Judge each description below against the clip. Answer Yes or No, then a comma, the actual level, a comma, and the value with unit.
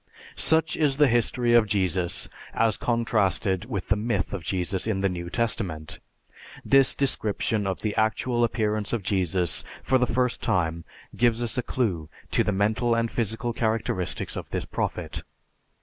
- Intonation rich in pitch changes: No, average, 3.8 semitones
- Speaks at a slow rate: No, average, 160 wpm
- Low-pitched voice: Yes, low, 110 Hz